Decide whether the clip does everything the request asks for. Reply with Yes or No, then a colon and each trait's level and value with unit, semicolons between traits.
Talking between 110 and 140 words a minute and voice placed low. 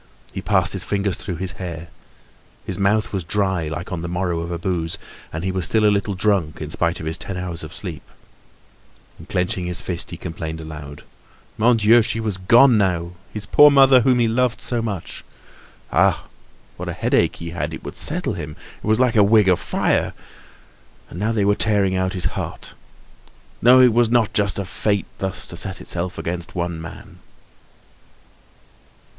No: average, 190 wpm; very low, 95 Hz